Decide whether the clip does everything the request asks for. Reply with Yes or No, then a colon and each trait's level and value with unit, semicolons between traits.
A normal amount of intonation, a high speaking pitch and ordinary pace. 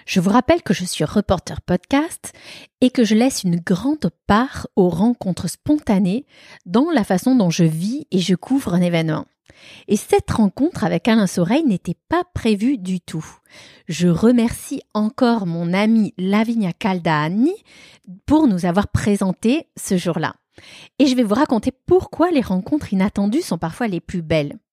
No: wide, 5.9 semitones; high, 205 Hz; average, 165 wpm